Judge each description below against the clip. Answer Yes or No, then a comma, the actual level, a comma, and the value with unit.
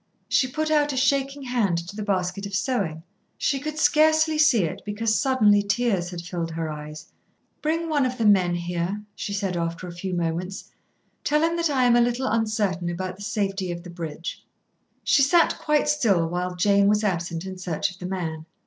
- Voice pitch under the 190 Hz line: No, high, 200 Hz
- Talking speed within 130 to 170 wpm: No, average, 200 wpm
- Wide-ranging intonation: Yes, wide, 6.8 semitones